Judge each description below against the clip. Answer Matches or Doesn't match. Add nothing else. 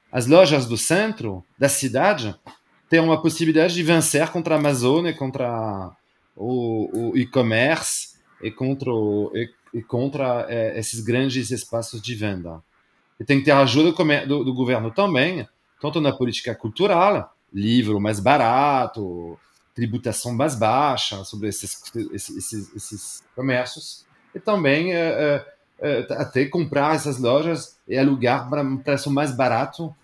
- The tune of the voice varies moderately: Matches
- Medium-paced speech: Matches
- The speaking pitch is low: Matches